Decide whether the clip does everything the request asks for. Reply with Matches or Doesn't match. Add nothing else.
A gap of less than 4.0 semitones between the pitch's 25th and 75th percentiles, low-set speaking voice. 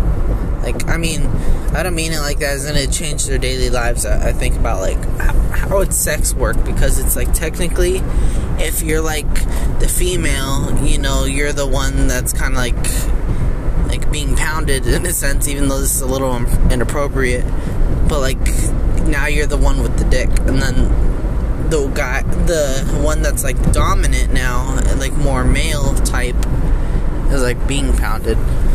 Matches